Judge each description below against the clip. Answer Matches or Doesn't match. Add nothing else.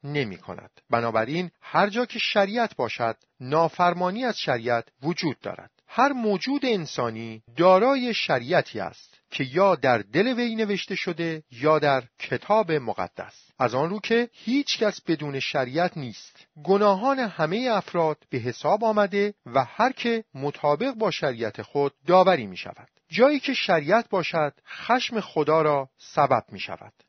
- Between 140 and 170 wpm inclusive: Matches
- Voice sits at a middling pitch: Matches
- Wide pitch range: Matches